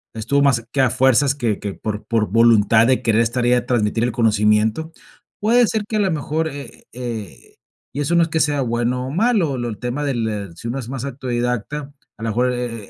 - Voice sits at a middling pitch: No, low, 125 Hz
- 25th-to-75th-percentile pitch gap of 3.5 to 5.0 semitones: Yes, average, 3.8 semitones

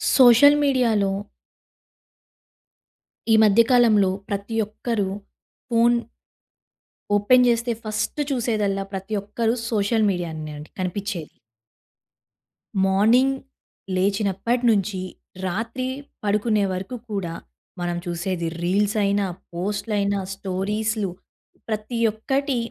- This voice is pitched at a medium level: No, high, 210 Hz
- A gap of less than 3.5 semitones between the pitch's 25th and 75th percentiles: Yes, average, 3.1 semitones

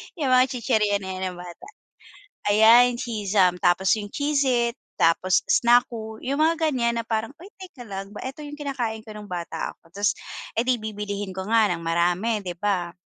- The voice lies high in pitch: Yes, high, 220 Hz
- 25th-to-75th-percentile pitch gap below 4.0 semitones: No, average, 4.5 semitones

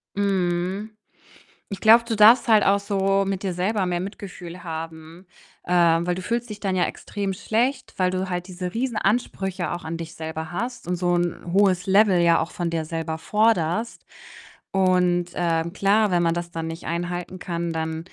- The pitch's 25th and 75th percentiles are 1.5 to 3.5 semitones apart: Yes, average, 2.8 semitones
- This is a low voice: No, medium, 180 Hz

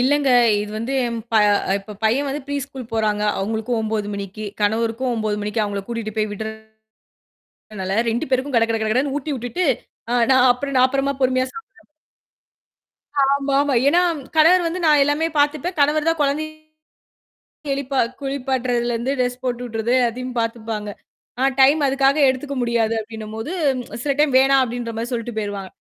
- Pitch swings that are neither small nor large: Yes, average, 3.9 semitones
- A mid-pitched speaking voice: No, very high, 250 Hz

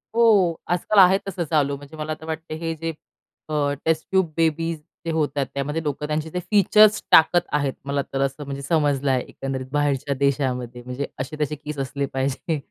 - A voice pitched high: No, medium, 150 Hz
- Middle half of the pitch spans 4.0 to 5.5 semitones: No, average, 2.7 semitones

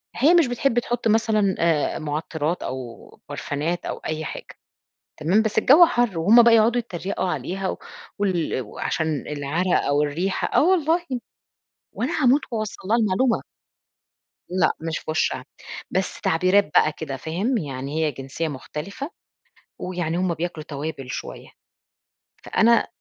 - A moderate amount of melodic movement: No, wide, 6.7 semitones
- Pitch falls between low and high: Yes, medium, 180 Hz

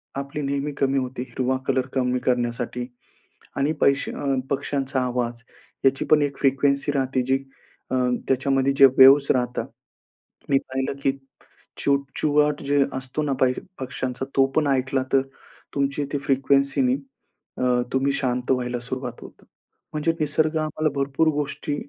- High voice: No, low, 135 Hz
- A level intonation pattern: Yes, narrow, 1.6 semitones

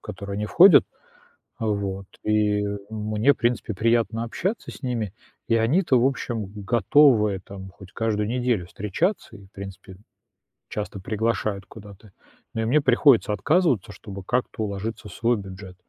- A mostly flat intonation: No, average, 3.1 semitones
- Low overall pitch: Yes, low, 110 Hz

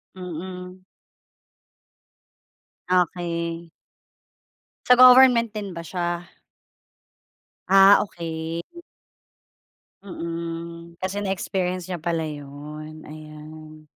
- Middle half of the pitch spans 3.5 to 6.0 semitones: No, narrow, 2.6 semitones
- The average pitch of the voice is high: No, medium, 170 Hz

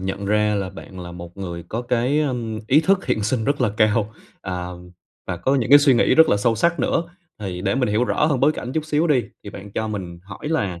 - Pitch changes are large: Yes, wide, 5.9 semitones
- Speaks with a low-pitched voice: Yes, low, 110 Hz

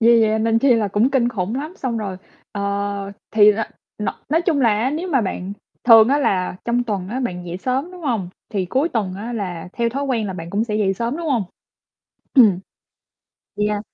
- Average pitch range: Yes, average, 4.3 semitones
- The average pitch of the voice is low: No, high, 225 Hz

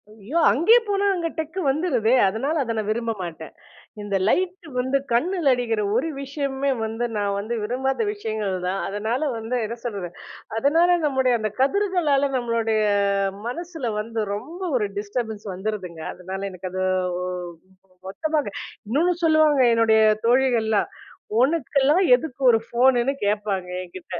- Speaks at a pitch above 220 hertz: Yes, high, 240 Hz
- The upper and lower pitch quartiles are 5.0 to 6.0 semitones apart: Yes, wide, 5.5 semitones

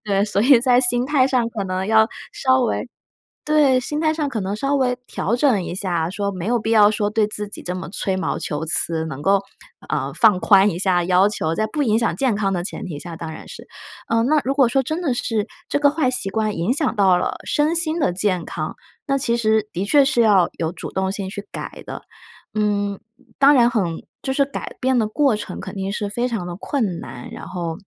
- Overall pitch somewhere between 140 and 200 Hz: No, high, 215 Hz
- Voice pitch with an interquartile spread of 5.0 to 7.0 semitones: Yes, average, 5.3 semitones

